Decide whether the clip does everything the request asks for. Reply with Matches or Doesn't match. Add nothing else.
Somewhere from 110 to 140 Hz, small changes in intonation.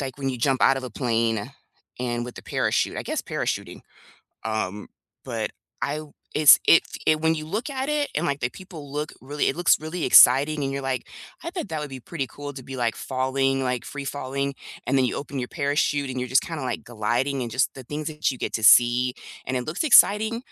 Doesn't match